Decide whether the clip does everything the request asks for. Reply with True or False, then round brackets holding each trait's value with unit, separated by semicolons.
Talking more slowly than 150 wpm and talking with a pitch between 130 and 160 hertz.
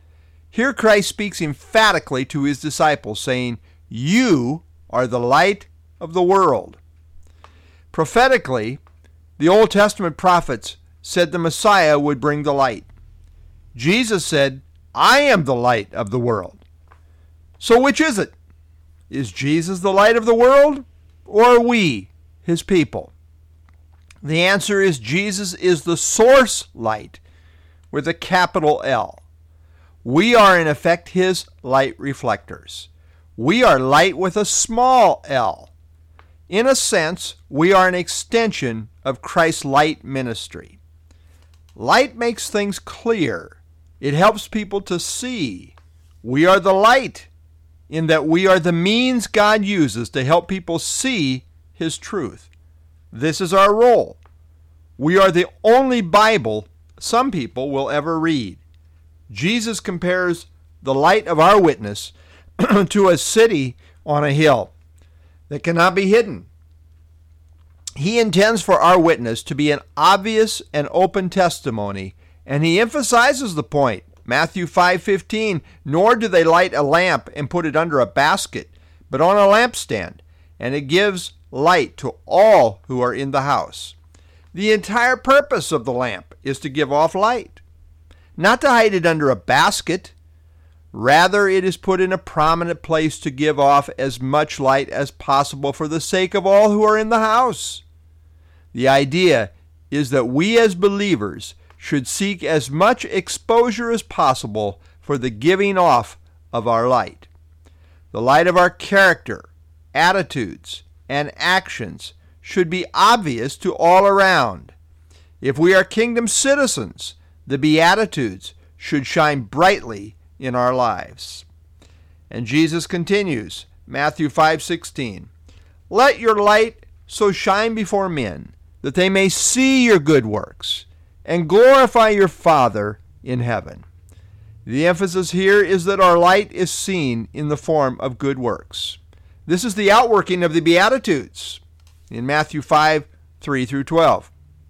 True (140 wpm; 140 Hz)